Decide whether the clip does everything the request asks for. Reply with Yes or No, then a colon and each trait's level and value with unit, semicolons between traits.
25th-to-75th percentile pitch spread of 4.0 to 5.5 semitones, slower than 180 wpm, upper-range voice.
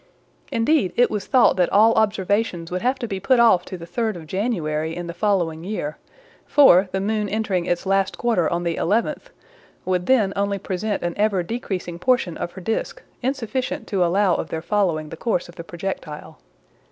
No: average, 4.3 semitones; average, 190 wpm; high, 195 Hz